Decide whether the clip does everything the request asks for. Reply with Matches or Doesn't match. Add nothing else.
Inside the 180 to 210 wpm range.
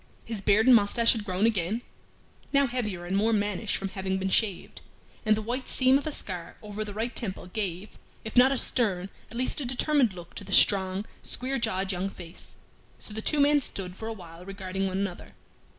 Matches